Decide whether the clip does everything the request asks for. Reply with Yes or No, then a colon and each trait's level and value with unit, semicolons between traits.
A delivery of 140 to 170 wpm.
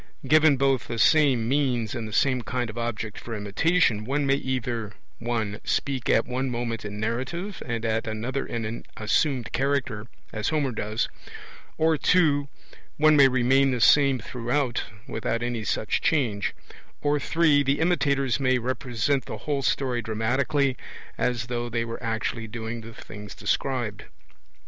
Yes: average, 155 wpm